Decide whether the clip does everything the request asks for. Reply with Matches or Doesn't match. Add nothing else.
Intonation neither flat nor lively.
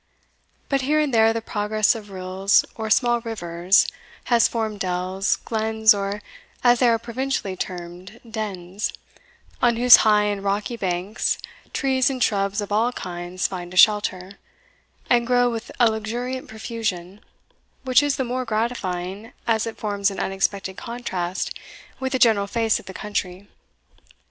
Matches